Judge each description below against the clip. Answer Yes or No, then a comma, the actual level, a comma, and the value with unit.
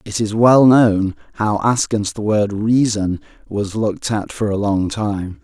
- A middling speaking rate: Yes, average, 175 wpm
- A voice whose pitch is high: No, low, 105 Hz